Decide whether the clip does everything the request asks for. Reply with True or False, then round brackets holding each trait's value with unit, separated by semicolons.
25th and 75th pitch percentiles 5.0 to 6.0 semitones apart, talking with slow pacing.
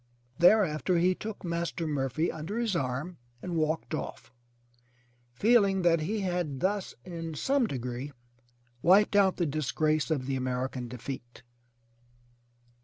True (5.4 semitones; 125 wpm)